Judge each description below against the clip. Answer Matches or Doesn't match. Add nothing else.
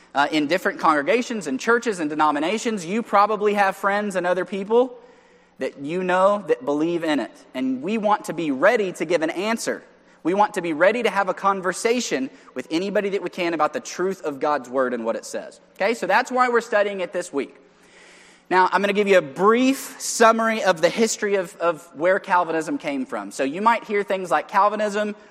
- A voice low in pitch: Doesn't match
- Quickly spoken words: Matches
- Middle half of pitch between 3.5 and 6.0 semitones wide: Matches